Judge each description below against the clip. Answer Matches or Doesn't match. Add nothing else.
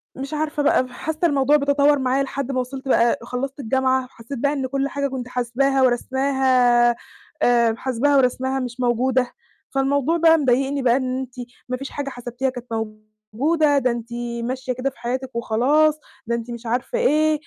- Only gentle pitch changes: Matches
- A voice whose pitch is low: Doesn't match